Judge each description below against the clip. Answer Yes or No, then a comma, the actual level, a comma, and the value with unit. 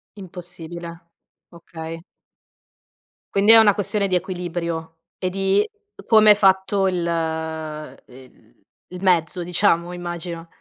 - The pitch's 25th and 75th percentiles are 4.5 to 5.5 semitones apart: No, average, 2.7 semitones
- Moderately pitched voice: Yes, medium, 175 Hz